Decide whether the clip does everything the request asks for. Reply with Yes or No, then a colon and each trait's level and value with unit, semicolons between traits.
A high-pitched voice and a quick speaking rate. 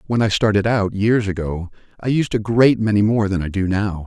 No: low, 105 Hz; fast, 235 wpm